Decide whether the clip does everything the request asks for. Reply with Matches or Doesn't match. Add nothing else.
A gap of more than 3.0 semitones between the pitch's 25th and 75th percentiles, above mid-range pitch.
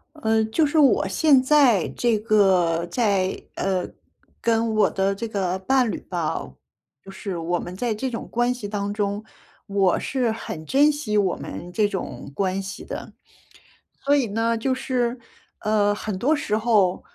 Matches